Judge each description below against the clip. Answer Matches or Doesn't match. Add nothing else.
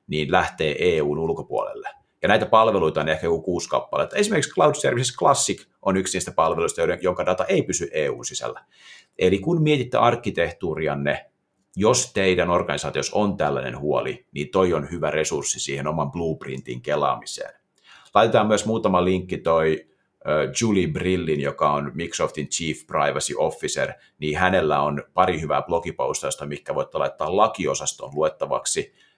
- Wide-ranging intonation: Matches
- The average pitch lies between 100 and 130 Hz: Doesn't match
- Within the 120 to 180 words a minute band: Matches